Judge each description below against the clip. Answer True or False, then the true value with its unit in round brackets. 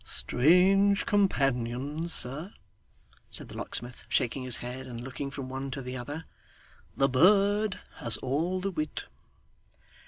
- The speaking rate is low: True (130 wpm)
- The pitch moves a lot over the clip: True (6.2 semitones)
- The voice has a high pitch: False (140 Hz)